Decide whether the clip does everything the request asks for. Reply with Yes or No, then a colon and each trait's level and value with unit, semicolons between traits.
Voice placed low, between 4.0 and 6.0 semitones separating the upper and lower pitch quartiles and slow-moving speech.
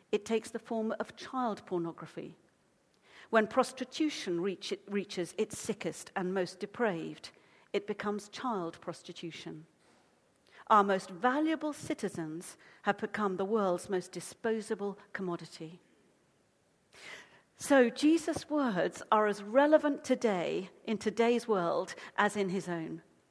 No: high, 205 Hz; average, 4.6 semitones; slow, 120 wpm